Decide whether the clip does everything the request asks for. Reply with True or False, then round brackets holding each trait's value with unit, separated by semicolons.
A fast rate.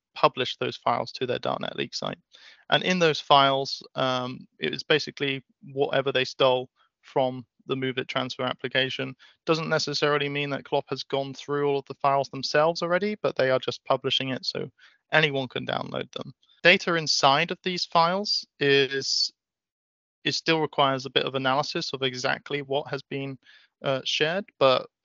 False (170 wpm)